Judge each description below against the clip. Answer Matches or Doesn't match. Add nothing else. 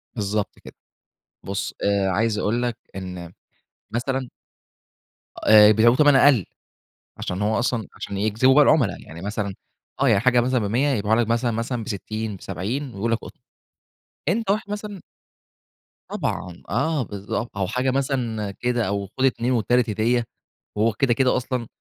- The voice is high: Doesn't match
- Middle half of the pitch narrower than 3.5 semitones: Doesn't match